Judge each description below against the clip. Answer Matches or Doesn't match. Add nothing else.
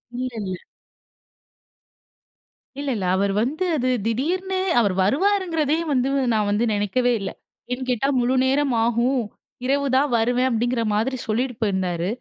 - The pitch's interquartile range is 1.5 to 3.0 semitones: Doesn't match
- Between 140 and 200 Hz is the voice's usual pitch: Doesn't match